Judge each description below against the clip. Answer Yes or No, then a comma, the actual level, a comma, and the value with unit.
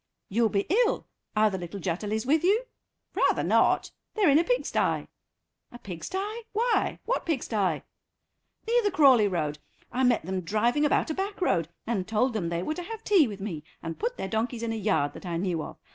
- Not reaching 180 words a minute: No, average, 200 wpm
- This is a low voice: No, high, 225 Hz